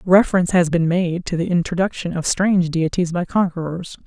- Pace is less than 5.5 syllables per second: No, 5.6 syllables/s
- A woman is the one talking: Yes, female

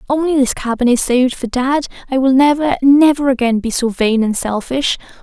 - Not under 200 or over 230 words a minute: Yes, fast, 205 wpm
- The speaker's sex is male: No, female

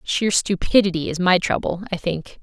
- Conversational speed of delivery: Yes, average, 175 wpm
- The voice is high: No, medium, 180 Hz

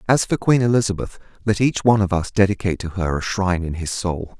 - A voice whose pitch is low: Yes, low, 100 Hz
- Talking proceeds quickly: Yes, fast, 230 wpm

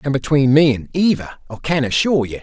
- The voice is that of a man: Yes, male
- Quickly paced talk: Yes, fast, 225 wpm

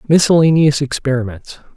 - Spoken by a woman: No, male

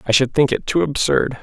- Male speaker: Yes, male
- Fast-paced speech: Yes, fast, 250 wpm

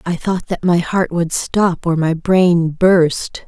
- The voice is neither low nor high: Yes, medium, 175 Hz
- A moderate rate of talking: Yes, average, 190 wpm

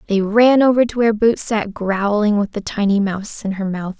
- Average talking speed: No, fast, 225 wpm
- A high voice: Yes, high, 210 Hz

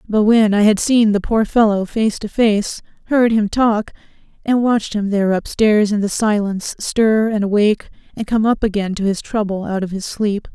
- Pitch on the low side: No, high, 210 Hz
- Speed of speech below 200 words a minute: No, fast, 205 wpm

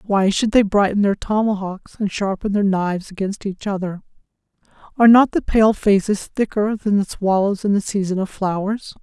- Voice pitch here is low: No, high, 200 Hz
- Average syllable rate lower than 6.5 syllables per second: Yes, 5.1 syllables/s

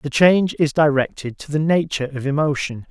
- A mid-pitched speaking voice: Yes, medium, 145 Hz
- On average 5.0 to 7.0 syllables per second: Yes, 5.7 syllables/s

